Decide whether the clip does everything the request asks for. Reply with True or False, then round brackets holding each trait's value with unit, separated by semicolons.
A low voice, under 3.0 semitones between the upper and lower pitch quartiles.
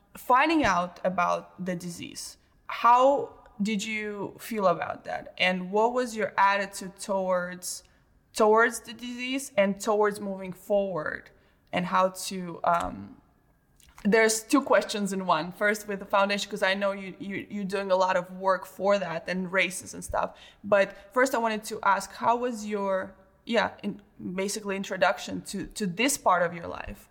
False (200 Hz; 2.6 semitones)